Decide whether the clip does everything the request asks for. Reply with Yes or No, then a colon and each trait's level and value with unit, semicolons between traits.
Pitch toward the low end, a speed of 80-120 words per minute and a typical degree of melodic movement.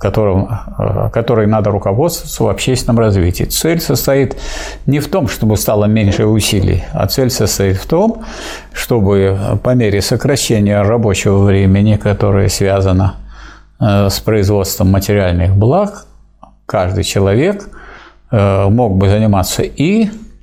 Yes: low, 105 Hz; average, 115 wpm; average, 4.2 semitones